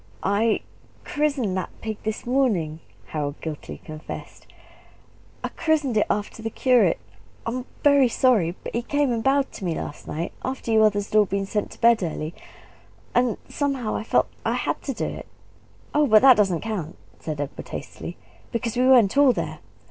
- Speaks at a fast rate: No, average, 180 wpm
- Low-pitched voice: No, high, 220 Hz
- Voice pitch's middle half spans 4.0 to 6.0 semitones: Yes, average, 5.0 semitones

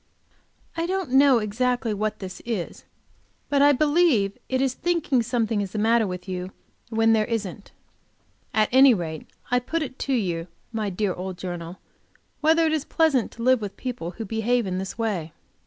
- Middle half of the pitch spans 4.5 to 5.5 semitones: Yes, average, 5.2 semitones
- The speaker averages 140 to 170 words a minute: No, average, 180 wpm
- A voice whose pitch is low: No, high, 225 Hz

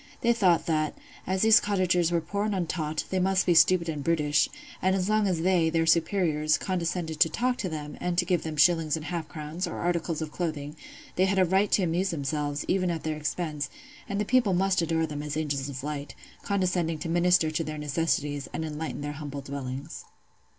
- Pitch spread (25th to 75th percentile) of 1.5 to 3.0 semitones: No, average, 3.4 semitones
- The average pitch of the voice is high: No, medium, 165 Hz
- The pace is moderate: No, fast, 210 wpm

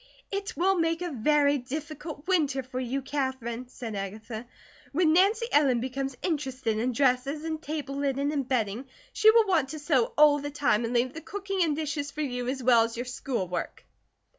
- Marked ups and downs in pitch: No, average, 3.8 semitones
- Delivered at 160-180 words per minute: No, average, 190 wpm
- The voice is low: No, very high, 275 Hz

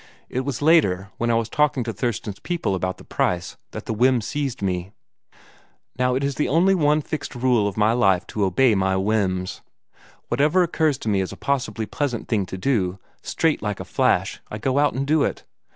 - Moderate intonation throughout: No, wide, 6.2 semitones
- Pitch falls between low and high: No, low, 120 Hz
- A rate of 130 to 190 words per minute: No, average, 200 wpm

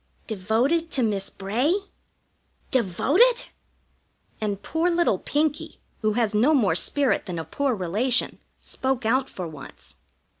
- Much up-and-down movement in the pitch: Yes, wide, 6.3 semitones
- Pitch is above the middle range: Yes, high, 240 Hz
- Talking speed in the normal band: No, slow, 125 wpm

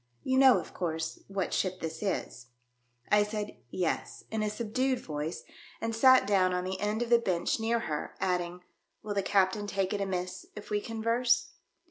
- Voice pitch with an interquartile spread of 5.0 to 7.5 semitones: No, average, 3.8 semitones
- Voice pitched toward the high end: Yes, high, 200 Hz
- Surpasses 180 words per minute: Yes, average, 190 wpm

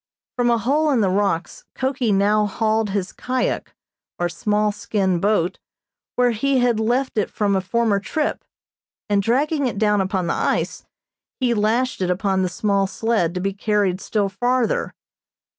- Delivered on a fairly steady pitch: No, average, 3.7 semitones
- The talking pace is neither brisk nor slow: Yes, average, 165 wpm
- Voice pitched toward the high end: Yes, high, 210 Hz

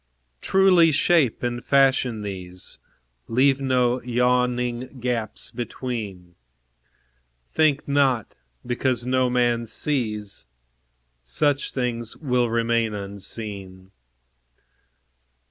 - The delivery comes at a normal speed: No, slow, 80 wpm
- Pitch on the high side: No, low, 120 Hz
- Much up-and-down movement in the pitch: No, average, 3.1 semitones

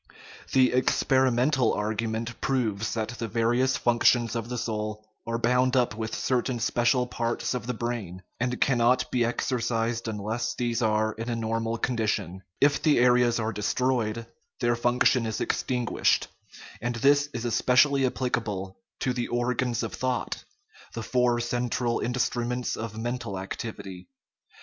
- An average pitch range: No, narrow, 1.9 semitones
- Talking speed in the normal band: Yes, average, 150 wpm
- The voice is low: Yes, low, 120 Hz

